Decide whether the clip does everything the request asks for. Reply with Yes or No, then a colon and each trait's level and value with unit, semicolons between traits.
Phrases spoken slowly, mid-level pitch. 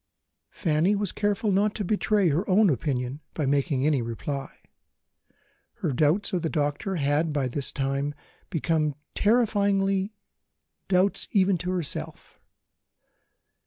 Yes: slow, 125 wpm; medium, 165 Hz